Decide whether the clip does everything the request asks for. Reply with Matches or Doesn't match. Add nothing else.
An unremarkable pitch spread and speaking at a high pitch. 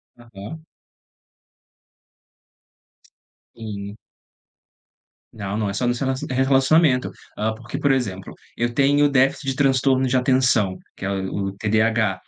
Doesn't match